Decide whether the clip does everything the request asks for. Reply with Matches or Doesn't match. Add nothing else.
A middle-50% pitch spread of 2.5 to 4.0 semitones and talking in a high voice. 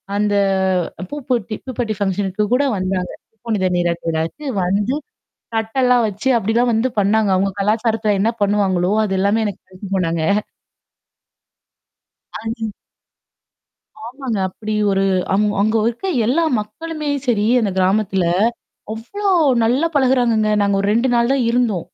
Matches